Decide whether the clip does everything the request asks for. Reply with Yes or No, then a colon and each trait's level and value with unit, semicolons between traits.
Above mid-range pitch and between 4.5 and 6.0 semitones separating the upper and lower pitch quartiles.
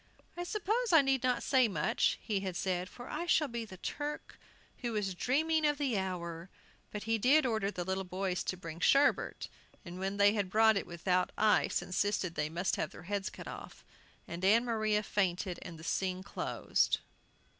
Yes: high, 205 Hz; average, 5.2 semitones